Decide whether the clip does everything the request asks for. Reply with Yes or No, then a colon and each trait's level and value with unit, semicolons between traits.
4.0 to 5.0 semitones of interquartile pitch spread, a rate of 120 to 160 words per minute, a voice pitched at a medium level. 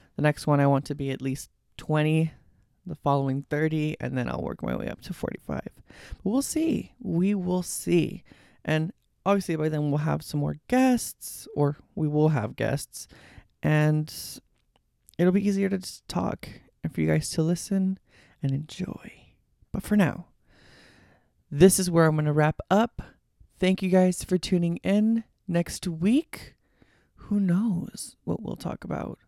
No: average, 4.7 semitones; average, 170 wpm; medium, 165 Hz